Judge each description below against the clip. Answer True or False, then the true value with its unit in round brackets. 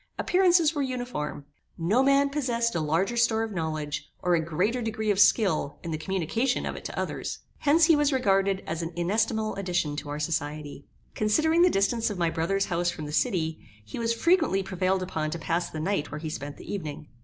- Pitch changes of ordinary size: False (6.7 semitones)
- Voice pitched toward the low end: False (190 Hz)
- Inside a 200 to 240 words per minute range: True (205 wpm)